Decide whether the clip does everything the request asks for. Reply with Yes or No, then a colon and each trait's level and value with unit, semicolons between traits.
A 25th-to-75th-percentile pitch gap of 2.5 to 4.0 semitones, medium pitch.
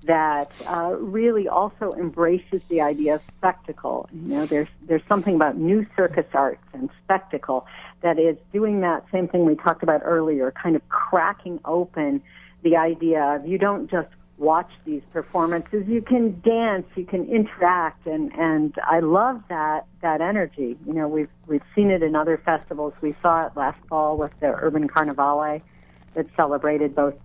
Yes: average, 3.3 semitones; medium, 165 Hz